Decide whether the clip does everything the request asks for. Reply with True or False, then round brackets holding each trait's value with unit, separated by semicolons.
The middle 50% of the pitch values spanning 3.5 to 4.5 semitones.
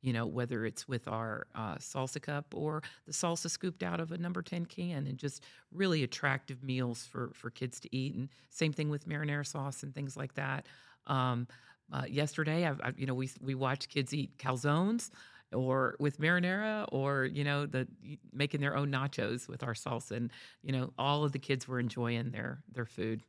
False (2.7 semitones)